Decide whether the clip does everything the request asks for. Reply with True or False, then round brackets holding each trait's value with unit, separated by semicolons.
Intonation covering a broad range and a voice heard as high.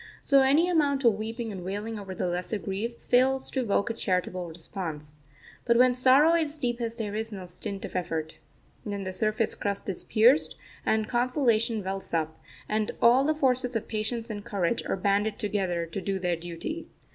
False (4.5 semitones; 215 Hz)